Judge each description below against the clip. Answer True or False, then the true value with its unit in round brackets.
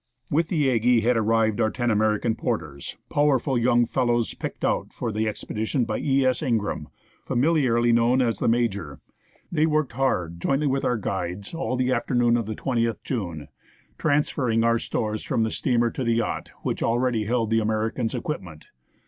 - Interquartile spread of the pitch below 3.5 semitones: True (2.8 semitones)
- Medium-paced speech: True (175 wpm)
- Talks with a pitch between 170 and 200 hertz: False (115 Hz)